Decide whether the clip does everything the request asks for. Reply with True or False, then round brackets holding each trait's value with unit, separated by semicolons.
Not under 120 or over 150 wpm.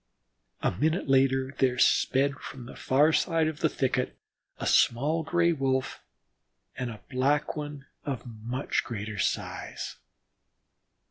True (135 wpm)